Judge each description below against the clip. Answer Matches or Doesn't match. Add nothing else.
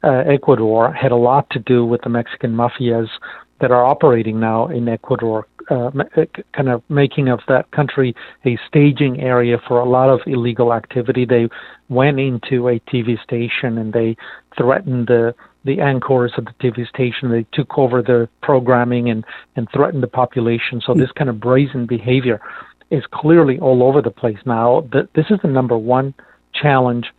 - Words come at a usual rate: Matches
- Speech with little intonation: Matches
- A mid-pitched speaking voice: Doesn't match